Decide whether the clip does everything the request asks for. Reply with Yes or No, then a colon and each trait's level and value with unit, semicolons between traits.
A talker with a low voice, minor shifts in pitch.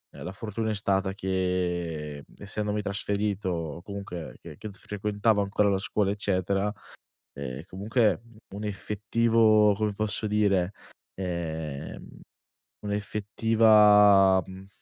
Yes: low, 100 Hz; narrow, 2.3 semitones